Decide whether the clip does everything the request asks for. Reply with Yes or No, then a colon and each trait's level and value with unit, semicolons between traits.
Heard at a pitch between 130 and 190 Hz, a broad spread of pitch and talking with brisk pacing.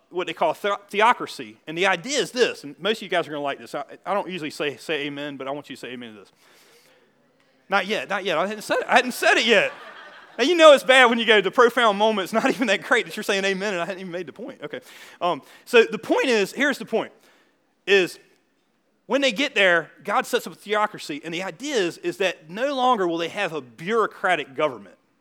No: high, 205 Hz; wide, 6.5 semitones; fast, 260 wpm